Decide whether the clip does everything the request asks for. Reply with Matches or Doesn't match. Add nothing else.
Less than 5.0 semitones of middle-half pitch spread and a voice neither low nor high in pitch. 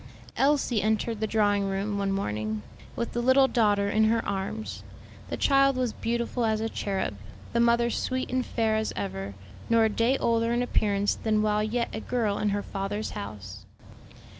Doesn't match